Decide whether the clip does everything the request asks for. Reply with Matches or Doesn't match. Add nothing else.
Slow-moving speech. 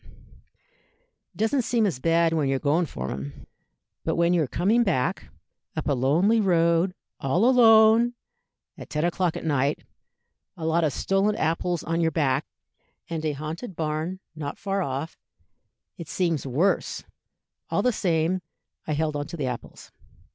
Doesn't match